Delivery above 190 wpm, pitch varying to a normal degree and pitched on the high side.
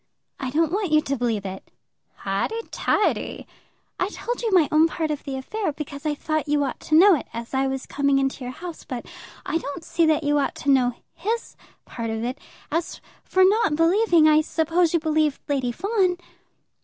Yes: average, 200 wpm; average, 4.2 semitones; very high, 305 Hz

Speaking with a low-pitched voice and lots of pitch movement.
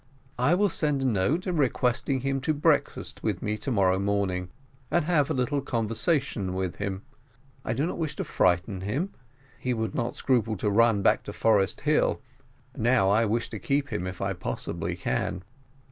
Yes: low, 115 Hz; wide, 6.0 semitones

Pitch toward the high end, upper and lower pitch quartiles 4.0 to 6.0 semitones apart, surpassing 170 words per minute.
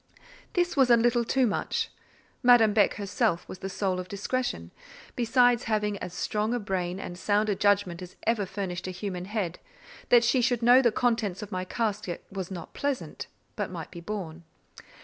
Yes: high, 210 Hz; average, 4.3 semitones; average, 185 wpm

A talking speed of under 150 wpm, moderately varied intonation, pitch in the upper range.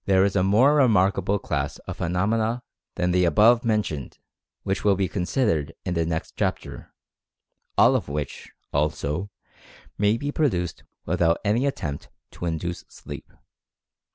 No: average, 140 wpm; average, 4.5 semitones; very low, 95 Hz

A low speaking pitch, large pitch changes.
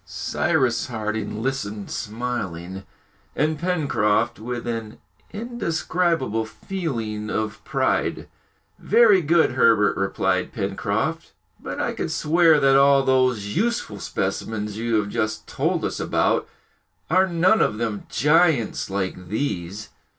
Yes: low, 120 Hz; wide, 6.9 semitones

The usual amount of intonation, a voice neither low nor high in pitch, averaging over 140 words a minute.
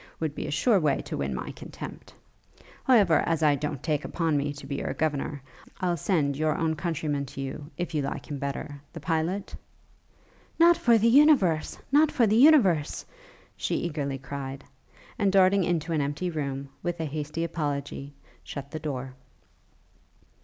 Yes: average, 4.0 semitones; medium, 155 Hz; average, 170 wpm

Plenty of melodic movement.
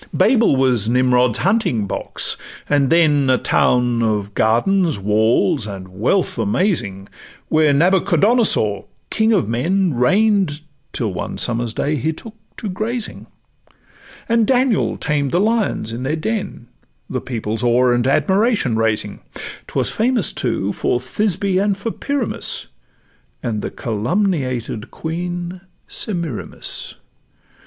Yes: wide, 9.0 semitones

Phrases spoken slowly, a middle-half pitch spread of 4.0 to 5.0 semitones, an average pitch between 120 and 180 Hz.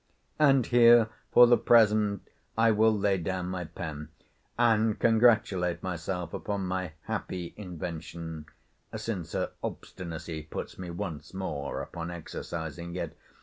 No: slow, 125 wpm; average, 4.4 semitones; very low, 90 Hz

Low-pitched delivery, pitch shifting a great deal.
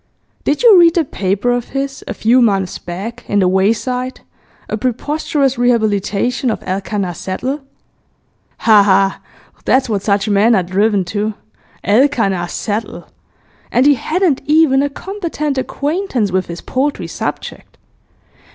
No: high, 230 Hz; wide, 5.7 semitones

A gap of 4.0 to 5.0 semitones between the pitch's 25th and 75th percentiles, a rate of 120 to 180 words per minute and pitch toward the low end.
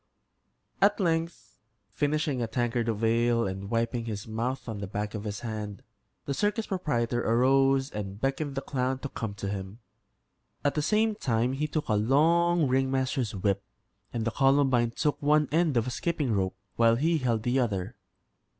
Yes: average, 4.7 semitones; average, 175 wpm; low, 125 Hz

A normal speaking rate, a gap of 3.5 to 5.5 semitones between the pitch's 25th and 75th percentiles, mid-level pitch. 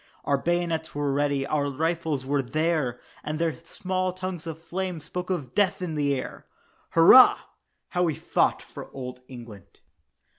Yes: average, 155 wpm; average, 3.8 semitones; medium, 160 Hz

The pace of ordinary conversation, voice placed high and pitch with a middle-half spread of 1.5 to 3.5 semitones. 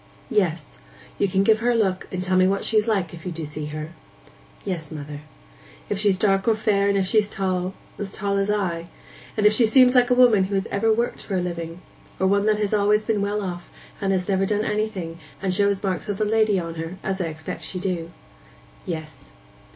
No: fast, 220 wpm; high, 195 Hz; average, 2.9 semitones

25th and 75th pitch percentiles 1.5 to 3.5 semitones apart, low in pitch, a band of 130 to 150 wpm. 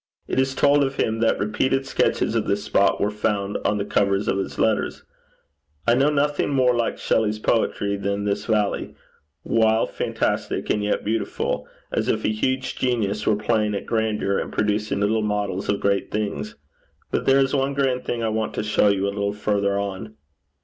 No: average, 3.1 semitones; low, 105 Hz; average, 190 wpm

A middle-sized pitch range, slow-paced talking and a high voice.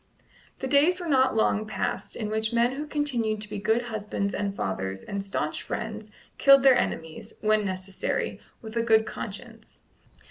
No: average, 3.5 semitones; average, 170 wpm; high, 220 Hz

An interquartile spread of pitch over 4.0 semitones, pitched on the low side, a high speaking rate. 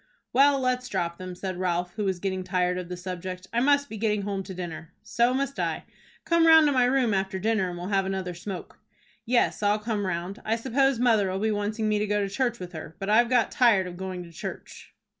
No: average, 4.5 semitones; high, 200 Hz; fast, 235 wpm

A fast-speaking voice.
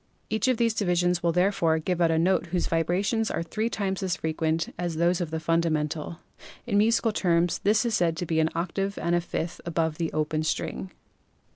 Yes: fast, 210 wpm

